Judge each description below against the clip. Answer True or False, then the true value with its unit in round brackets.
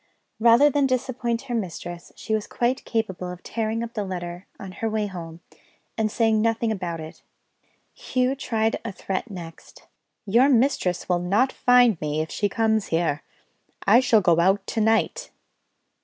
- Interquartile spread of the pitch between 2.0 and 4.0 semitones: False (4.7 semitones)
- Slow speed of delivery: False (165 wpm)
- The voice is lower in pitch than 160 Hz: False (220 Hz)